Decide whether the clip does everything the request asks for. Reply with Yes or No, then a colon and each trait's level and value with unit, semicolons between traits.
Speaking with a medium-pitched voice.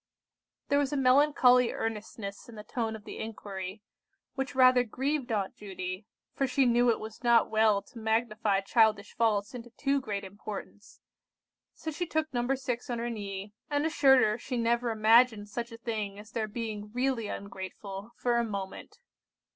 No: high, 230 Hz